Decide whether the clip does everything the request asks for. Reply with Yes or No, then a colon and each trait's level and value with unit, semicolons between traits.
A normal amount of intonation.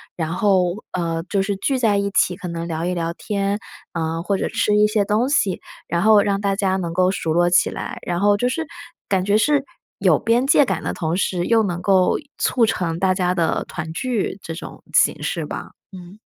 Yes: average, 3.1 semitones